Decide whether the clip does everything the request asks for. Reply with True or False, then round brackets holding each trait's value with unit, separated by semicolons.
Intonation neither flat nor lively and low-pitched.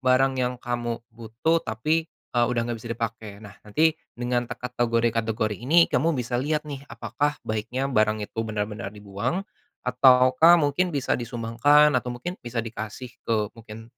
True (3.3 semitones; 120 Hz)